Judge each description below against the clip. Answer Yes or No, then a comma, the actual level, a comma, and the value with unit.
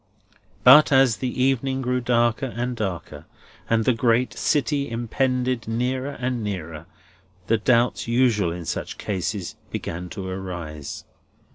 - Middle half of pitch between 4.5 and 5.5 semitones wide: Yes, average, 4.9 semitones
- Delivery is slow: Yes, slow, 130 wpm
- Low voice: Yes, low, 120 Hz